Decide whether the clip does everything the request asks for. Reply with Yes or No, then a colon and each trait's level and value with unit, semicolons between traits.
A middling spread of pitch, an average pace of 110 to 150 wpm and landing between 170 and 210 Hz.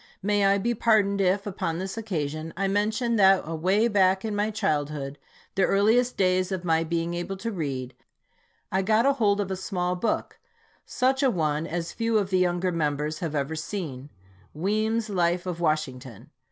No: average, 4.3 semitones; average, 180 wpm; medium, 185 Hz